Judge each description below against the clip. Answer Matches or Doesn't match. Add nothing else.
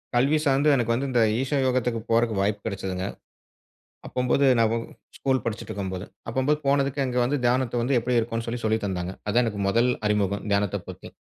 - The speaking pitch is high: Doesn't match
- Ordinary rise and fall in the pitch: Matches